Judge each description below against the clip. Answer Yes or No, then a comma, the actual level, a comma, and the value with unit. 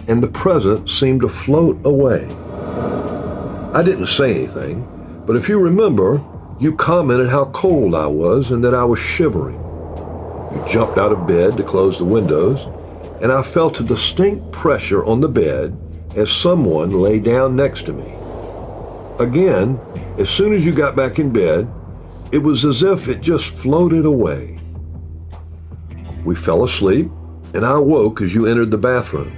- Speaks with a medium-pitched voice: No, low, 115 Hz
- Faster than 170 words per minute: No, average, 160 wpm